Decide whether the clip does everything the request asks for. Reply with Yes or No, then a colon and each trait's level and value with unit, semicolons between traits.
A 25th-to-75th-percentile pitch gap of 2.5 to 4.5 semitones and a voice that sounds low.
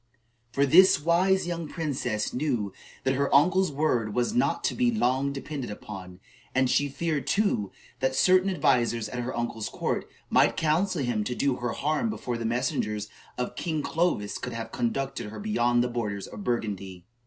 No: wide, 5.6 semitones; low, 130 Hz